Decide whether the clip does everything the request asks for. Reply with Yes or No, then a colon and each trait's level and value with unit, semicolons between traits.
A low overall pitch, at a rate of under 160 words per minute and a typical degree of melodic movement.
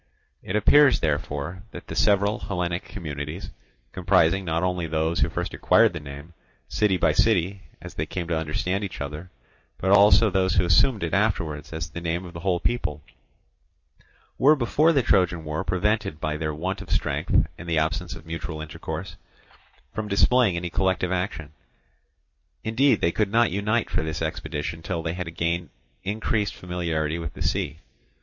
No: very low, 90 Hz; average, 170 wpm; average, 3.7 semitones